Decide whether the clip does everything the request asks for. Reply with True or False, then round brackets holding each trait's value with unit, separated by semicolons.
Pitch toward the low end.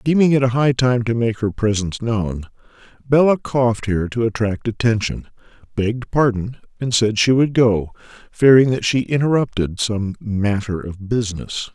True (115 Hz)